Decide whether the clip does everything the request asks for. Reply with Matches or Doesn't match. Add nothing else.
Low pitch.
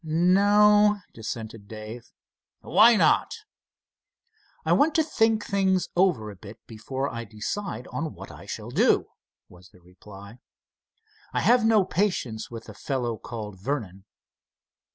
Matches